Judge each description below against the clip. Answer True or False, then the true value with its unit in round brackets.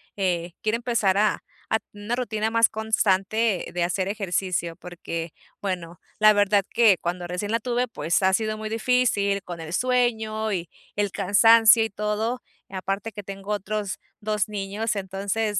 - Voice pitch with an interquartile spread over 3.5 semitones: False (2.8 semitones)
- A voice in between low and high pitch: False (205 Hz)